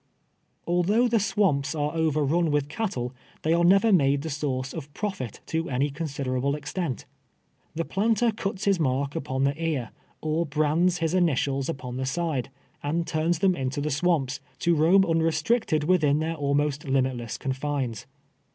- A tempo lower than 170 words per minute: Yes, average, 160 wpm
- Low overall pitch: No, medium, 155 Hz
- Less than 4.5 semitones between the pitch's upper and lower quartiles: Yes, average, 3.9 semitones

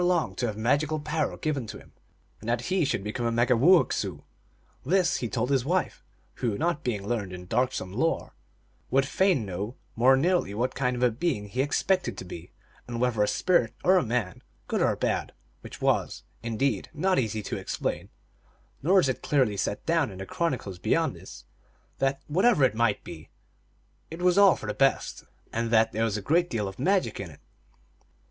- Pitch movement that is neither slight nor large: No, wide, 6.5 semitones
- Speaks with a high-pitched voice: No, low, 125 Hz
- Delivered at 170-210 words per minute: Yes, average, 195 wpm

